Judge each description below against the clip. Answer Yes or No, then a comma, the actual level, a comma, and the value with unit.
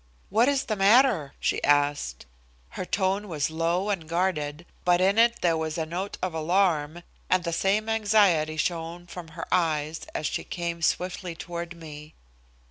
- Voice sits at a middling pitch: Yes, medium, 175 Hz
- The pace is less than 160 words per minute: No, average, 165 wpm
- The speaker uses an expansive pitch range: No, average, 3.4 semitones